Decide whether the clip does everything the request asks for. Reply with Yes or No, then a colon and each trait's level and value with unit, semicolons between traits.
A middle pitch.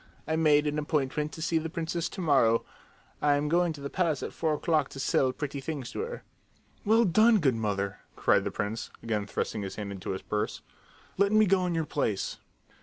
Yes: medium, 150 Hz